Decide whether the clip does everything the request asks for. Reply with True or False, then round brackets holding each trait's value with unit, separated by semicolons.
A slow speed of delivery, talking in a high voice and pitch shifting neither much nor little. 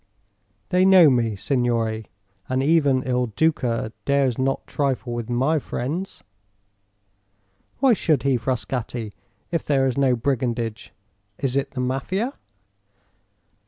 False (120 wpm; 130 Hz; 3.0 semitones)